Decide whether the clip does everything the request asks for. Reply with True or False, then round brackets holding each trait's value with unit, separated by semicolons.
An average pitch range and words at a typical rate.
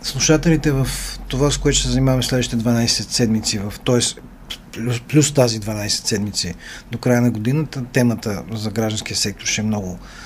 False (3.0 semitones; 170 wpm)